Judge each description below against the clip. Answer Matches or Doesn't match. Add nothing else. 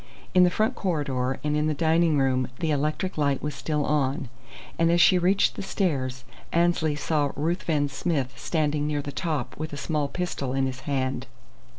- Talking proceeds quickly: Doesn't match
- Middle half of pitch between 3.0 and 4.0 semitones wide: Matches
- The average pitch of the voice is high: Doesn't match